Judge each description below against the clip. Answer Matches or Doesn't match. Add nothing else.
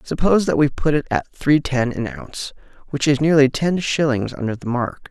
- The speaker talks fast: Matches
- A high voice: Doesn't match